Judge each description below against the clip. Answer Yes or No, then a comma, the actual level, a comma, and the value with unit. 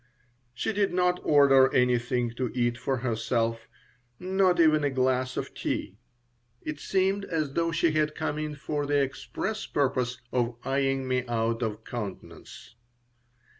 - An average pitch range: Yes, average, 4.2 semitones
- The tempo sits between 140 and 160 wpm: Yes, average, 145 wpm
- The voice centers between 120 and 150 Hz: Yes, low, 135 Hz